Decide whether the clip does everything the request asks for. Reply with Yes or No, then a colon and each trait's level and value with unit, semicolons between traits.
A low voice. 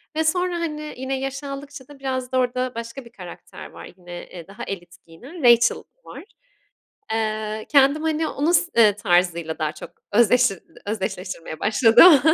No: high, 245 Hz